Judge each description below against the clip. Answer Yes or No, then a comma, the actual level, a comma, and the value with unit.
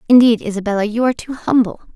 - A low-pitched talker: No, high, 225 Hz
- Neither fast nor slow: Yes, average, 185 wpm